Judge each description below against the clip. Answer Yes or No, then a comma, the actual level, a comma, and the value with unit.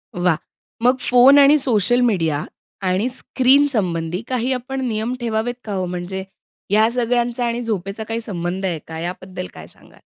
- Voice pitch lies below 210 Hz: No, high, 220 Hz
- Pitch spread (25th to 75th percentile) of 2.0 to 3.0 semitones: No, average, 5.1 semitones